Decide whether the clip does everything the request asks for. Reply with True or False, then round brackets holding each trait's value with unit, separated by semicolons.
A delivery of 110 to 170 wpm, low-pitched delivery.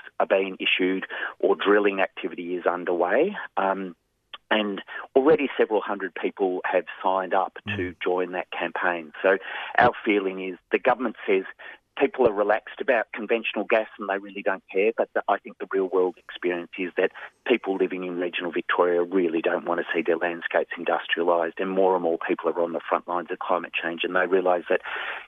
False (190 wpm; 95 Hz)